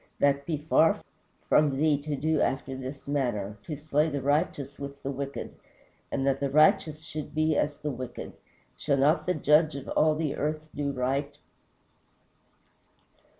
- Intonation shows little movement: Yes, narrow, 1.9 semitones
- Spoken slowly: No, average, 160 wpm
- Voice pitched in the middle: Yes, medium, 145 Hz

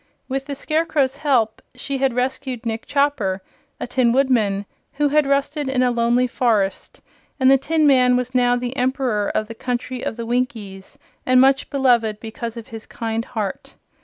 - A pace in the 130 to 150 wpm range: No, average, 175 wpm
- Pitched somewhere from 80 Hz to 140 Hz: No, very high, 250 Hz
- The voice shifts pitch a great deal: No, average, 2.9 semitones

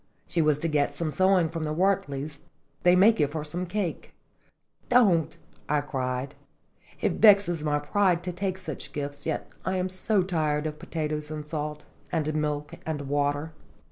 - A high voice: No, medium, 155 Hz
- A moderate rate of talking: Yes, average, 170 wpm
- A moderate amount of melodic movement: Yes, average, 3.6 semitones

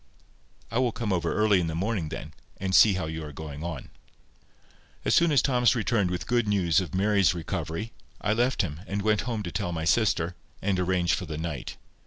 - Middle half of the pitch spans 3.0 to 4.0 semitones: No, average, 4.7 semitones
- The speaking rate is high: Yes, fast, 210 wpm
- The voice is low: Yes, very low, 95 Hz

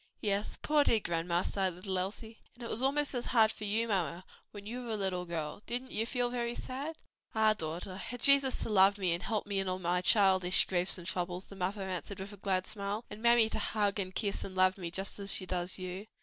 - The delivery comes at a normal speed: No, fast, 245 wpm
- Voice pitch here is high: Yes, high, 200 Hz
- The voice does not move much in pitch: No, average, 3.4 semitones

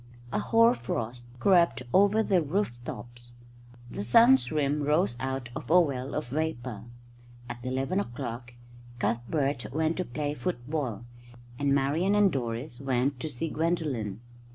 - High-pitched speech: No, medium, 140 Hz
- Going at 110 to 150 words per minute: Yes, average, 140 wpm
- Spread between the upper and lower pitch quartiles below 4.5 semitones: No, average, 5.3 semitones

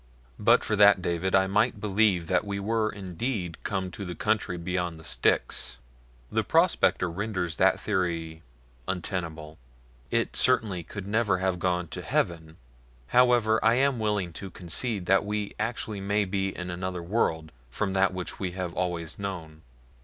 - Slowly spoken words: No, average, 160 wpm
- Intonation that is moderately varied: Yes, average, 3.2 semitones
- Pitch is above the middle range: No, very low, 95 Hz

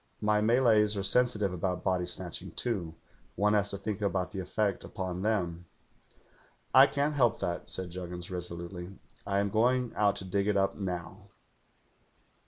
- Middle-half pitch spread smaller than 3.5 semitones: Yes, average, 2.9 semitones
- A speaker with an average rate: Yes, average, 165 wpm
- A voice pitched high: No, low, 100 Hz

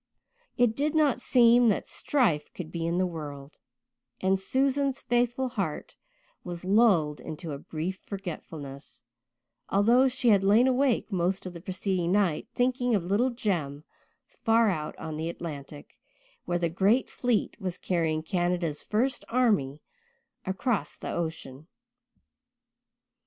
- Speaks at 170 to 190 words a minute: No, slow, 135 wpm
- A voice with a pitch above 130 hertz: Yes, high, 190 Hz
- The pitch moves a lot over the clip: Yes, wide, 6.7 semitones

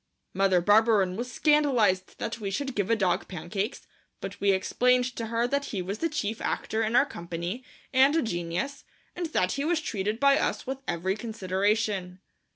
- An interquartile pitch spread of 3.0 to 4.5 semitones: No, average, 5.3 semitones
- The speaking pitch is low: No, high, 220 Hz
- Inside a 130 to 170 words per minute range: No, average, 180 wpm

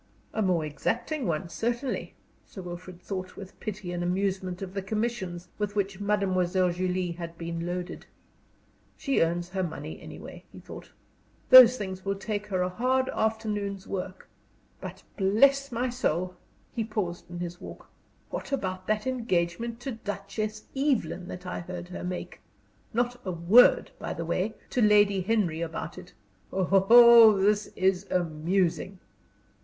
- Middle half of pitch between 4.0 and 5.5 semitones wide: No, average, 3.5 semitones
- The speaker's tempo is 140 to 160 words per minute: Yes, average, 150 wpm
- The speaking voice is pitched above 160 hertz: Yes, high, 190 Hz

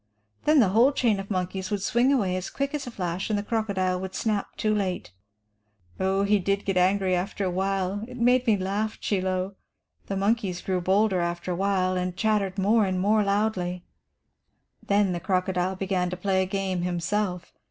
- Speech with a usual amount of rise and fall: No, narrow, 2.3 semitones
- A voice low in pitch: No, high, 195 Hz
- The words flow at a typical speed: Yes, average, 190 wpm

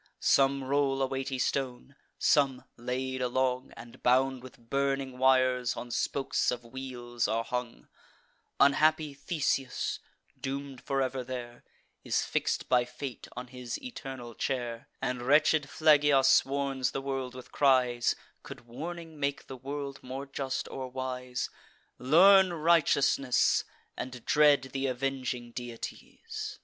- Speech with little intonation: Yes, narrow, 1.8 semitones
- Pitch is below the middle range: Yes, low, 130 Hz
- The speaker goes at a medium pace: No, slow, 130 wpm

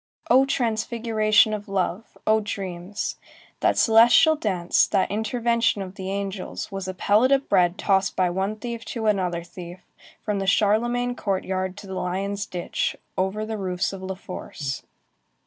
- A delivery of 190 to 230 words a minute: No, average, 155 wpm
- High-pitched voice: Yes, high, 200 Hz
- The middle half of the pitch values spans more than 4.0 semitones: No, average, 2.8 semitones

